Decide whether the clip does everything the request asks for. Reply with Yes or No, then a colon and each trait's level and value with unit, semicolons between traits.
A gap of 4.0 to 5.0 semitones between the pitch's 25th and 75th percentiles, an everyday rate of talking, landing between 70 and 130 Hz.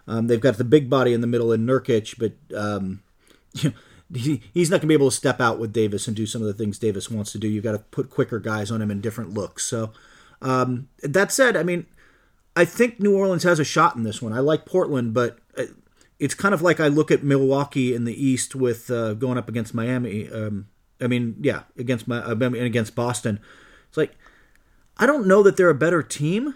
No: average, 4.7 semitones; fast, 235 wpm; low, 125 Hz